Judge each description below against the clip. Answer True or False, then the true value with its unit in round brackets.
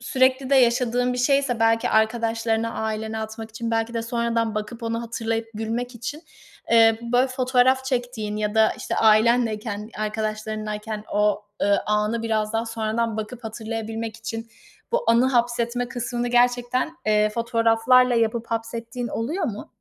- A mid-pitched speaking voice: False (230 Hz)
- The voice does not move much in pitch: True (1.8 semitones)